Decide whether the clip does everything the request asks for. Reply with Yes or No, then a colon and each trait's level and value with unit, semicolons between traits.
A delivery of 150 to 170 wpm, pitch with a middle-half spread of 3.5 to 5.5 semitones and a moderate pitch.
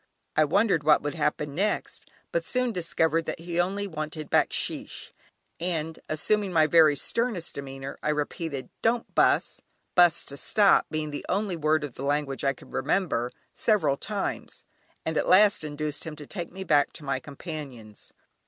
Yes: average, 165 wpm; average, 4.0 semitones; medium, 155 Hz